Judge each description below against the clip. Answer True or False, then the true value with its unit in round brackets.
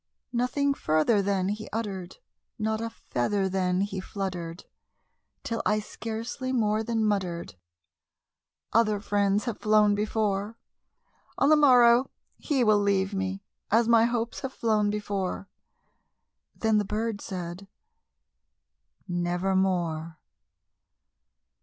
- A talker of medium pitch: False (210 Hz)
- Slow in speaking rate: True (110 wpm)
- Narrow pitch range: False (3.0 semitones)